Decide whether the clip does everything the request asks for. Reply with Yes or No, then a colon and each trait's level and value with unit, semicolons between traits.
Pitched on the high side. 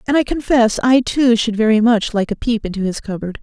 Yes: high, 225 Hz